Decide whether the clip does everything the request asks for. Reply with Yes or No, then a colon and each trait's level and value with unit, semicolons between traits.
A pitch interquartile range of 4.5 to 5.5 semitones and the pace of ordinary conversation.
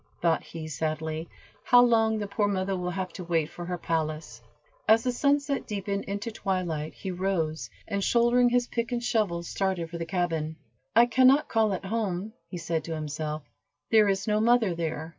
Yes: average, 5.2 semitones; average, 190 wpm